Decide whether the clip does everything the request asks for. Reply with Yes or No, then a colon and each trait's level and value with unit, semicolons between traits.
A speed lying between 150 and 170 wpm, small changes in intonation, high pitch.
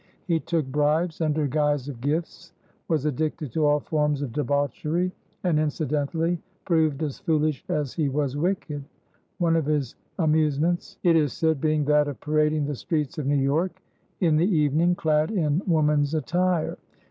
No: average, 160 wpm; narrow, 2.0 semitones; medium, 155 Hz